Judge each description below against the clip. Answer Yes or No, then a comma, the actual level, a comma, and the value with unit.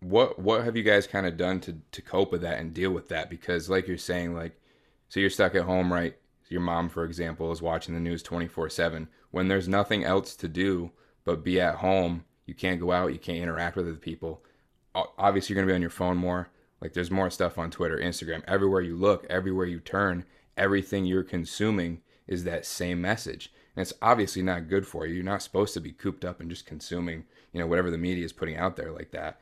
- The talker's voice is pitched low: Yes, very low, 90 Hz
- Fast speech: Yes, fast, 235 wpm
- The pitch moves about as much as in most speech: No, narrow, 1.9 semitones